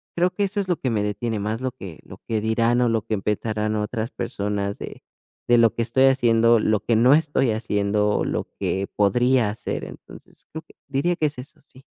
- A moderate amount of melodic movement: Yes, average, 3.6 semitones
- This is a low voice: Yes, low, 115 Hz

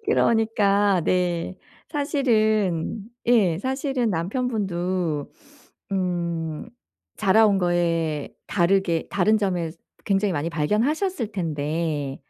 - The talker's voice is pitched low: No, high, 190 Hz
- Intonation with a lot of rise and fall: No, average, 4.5 semitones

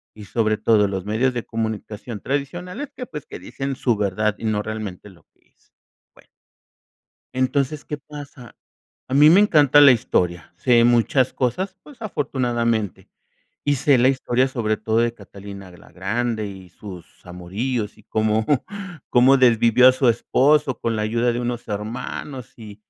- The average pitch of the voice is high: No, low, 120 Hz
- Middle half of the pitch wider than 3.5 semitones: Yes, average, 3.9 semitones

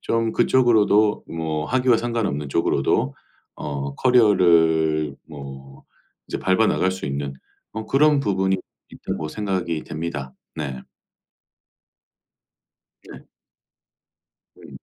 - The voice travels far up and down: Yes, wide, 6.9 semitones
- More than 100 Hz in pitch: No, very low, 85 Hz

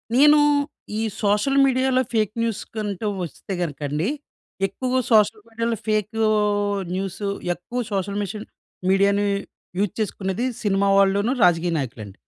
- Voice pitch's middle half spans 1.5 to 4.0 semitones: Yes, average, 2.9 semitones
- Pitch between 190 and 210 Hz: Yes, high, 205 Hz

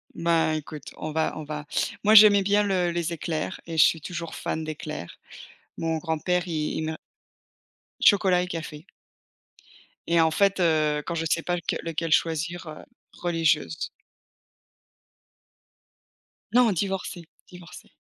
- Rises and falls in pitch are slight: Yes, narrow, 2.3 semitones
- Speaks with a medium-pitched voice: Yes, medium, 165 Hz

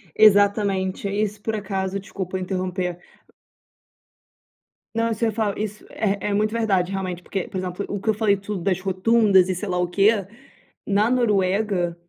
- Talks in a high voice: Yes, high, 200 Hz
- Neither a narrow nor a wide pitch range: No, narrow, 2.3 semitones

